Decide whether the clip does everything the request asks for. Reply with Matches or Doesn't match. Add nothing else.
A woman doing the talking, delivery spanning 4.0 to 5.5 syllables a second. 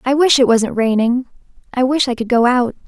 Matches